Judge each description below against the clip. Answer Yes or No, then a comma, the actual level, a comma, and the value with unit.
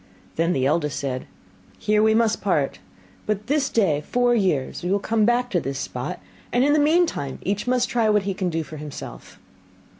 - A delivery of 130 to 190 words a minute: No, average, 200 wpm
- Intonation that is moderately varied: No, wide, 7.7 semitones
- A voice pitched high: Yes, high, 205 Hz